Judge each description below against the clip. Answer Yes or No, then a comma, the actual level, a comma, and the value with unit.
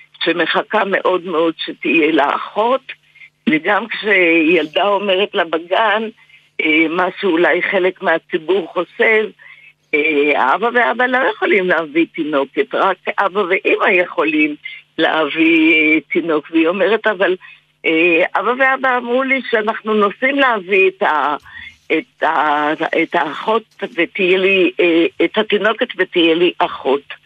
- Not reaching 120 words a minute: Yes, average, 110 wpm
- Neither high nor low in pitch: No, high, 195 Hz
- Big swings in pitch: Yes, wide, 6.4 semitones